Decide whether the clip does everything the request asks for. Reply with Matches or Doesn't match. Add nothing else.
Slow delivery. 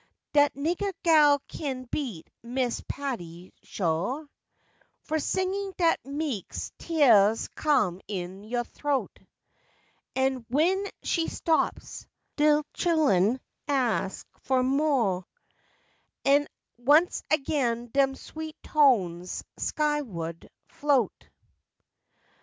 Matches